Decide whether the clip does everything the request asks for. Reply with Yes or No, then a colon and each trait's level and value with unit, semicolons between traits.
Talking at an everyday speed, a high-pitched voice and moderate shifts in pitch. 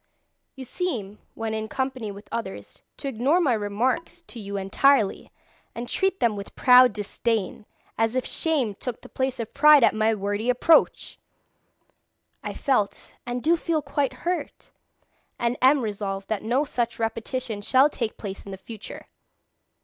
Yes: average, 155 wpm; high, 235 Hz; average, 4.2 semitones